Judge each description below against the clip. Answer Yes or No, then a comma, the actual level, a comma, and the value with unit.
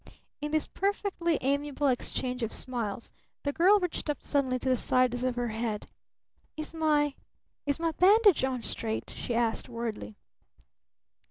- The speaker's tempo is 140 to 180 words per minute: Yes, average, 150 wpm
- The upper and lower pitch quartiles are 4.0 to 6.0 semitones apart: Yes, average, 4.6 semitones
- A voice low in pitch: No, very high, 265 Hz